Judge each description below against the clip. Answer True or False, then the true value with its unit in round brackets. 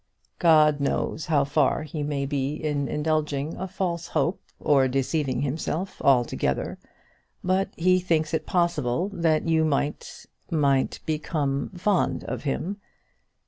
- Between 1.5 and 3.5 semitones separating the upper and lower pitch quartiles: True (3.1 semitones)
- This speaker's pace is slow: True (125 wpm)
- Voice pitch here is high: False (155 Hz)